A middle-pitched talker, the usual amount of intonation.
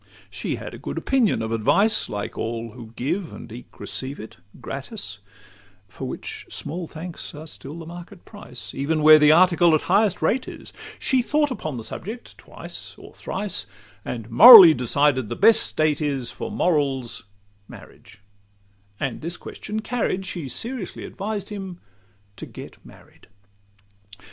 No: medium, 160 Hz; wide, 7.6 semitones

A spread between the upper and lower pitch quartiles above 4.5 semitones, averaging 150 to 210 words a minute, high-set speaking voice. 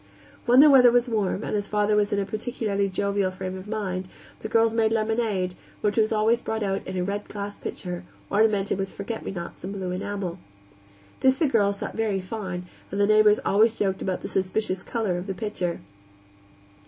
No: narrow, 2.6 semitones; average, 200 wpm; high, 205 Hz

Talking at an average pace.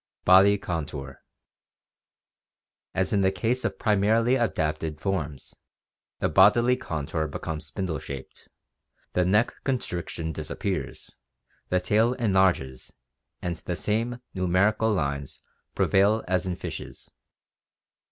No: slow, 115 wpm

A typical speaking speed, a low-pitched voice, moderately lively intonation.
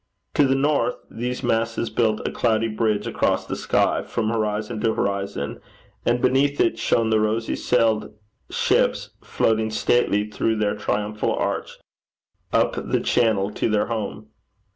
No: average, 145 wpm; low, 110 Hz; narrow, 1.8 semitones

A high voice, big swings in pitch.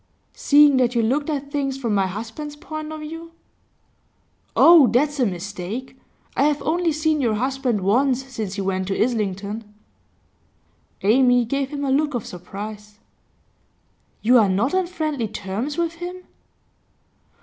Yes: very high, 260 Hz; wide, 6.0 semitones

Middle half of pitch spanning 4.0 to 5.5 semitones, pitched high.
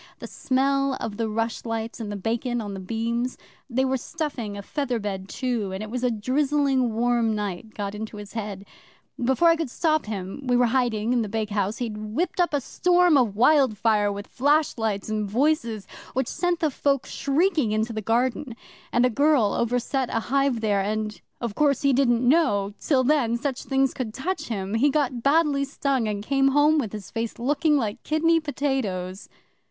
Yes: average, 4.4 semitones; high, 240 Hz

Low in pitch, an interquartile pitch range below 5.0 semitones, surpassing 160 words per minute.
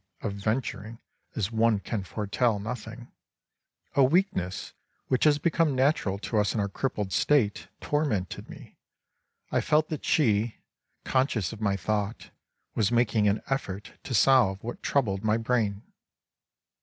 No: low, 110 Hz; average, 4.3 semitones; average, 145 wpm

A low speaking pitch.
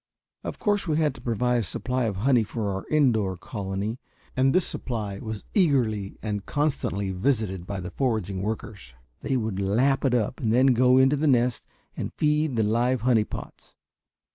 Yes: low, 115 Hz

